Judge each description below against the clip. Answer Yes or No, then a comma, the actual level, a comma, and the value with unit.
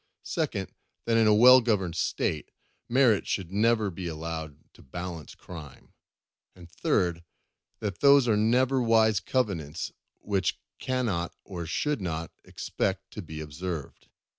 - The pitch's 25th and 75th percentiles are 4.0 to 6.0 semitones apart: Yes, wide, 5.5 semitones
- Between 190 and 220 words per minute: No, average, 140 wpm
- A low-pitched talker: Yes, very low, 95 Hz